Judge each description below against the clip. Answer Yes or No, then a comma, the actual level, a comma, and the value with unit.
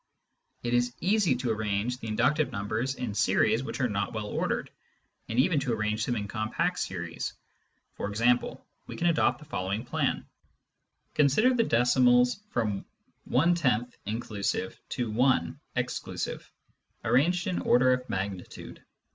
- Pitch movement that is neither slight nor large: Yes, average, 3.7 semitones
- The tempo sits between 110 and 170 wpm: Yes, average, 140 wpm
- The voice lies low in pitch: Yes, low, 120 Hz